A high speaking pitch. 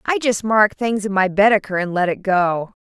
Yes: high, 200 Hz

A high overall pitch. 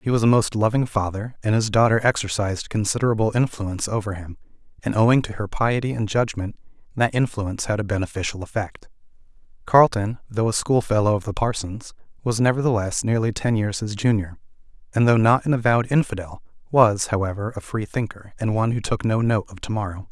No: low, 110 Hz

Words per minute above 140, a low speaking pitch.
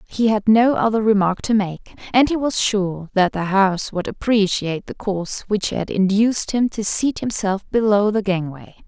No: average, 190 wpm; high, 205 Hz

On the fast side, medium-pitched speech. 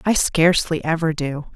No: average, 155 wpm; medium, 160 Hz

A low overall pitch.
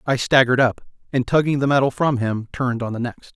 Yes: low, 130 Hz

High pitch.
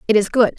Yes: high, 220 Hz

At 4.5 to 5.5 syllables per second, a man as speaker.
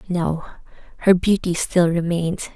No: 4.9 syllables/s; female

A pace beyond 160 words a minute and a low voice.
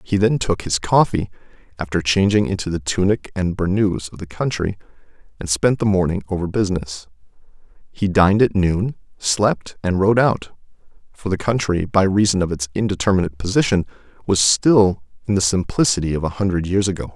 Yes: average, 170 wpm; very low, 95 Hz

